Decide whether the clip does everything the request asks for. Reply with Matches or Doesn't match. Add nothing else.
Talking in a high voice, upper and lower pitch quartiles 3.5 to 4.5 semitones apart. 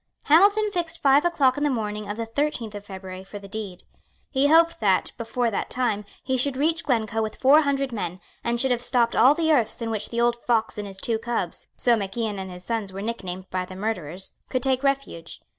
Doesn't match